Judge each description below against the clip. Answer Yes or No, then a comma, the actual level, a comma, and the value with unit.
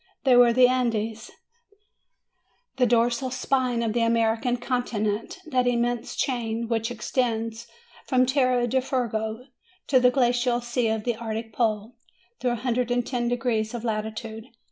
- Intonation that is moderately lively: No, narrow, 1.9 semitones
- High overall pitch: Yes, high, 240 Hz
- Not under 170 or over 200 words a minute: No, average, 145 wpm